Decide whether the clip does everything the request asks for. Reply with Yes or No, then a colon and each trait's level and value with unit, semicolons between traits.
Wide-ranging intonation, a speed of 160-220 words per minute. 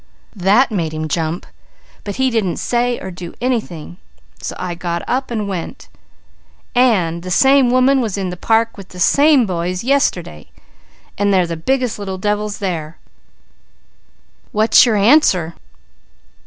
No: wide, 5.7 semitones; average, 145 wpm